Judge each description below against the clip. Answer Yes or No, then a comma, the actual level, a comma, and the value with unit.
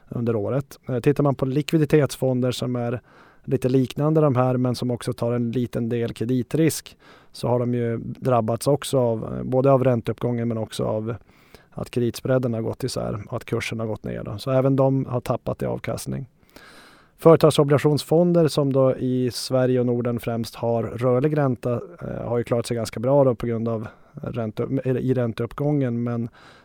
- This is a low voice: Yes, low, 125 Hz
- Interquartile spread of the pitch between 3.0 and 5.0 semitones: No, narrow, 2.4 semitones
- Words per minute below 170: No, average, 175 wpm